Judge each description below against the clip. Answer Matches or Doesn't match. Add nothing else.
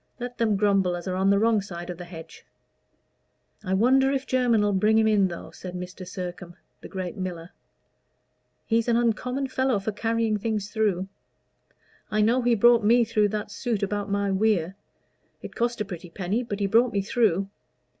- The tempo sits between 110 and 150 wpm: Doesn't match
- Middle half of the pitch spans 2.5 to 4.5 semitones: Matches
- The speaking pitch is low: Doesn't match